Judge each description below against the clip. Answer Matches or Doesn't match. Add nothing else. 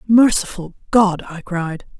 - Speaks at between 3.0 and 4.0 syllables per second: Matches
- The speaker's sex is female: Matches